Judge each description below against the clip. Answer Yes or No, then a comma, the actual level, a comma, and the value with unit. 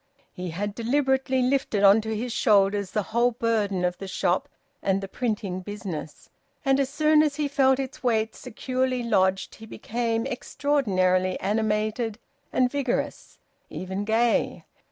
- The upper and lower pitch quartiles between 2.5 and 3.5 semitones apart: No, average, 4.6 semitones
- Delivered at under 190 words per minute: Yes, average, 145 wpm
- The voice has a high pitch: Yes, high, 225 Hz